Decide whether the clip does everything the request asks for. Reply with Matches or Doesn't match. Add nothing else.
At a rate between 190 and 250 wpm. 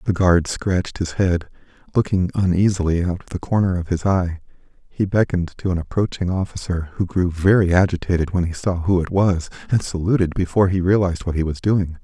Matches